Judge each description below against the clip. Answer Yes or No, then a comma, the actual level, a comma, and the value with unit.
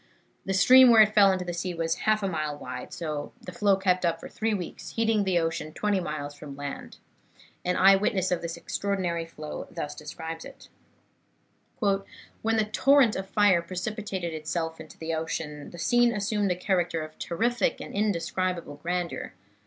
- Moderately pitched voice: Yes, medium, 180 Hz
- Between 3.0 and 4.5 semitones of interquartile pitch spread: Yes, average, 4.1 semitones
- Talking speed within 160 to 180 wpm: Yes, average, 175 wpm